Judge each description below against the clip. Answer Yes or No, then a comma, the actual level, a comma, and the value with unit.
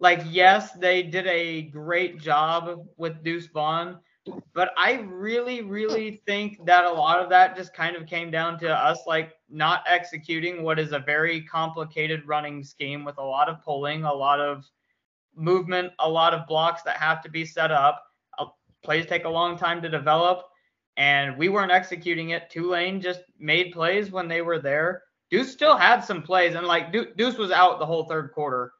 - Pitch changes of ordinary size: No, narrow, 2.3 semitones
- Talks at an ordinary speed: Yes, average, 190 wpm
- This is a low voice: No, medium, 170 Hz